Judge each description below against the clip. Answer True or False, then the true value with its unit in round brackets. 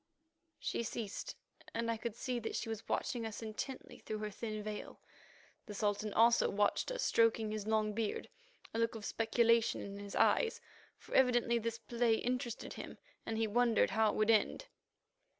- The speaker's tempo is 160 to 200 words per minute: True (175 wpm)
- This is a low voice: False (225 Hz)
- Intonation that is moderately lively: False (1.6 semitones)